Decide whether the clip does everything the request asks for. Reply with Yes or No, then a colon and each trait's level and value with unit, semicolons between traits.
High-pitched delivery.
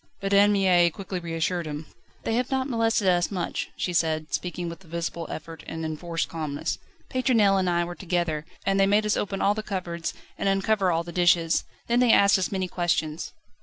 No: medium, 180 Hz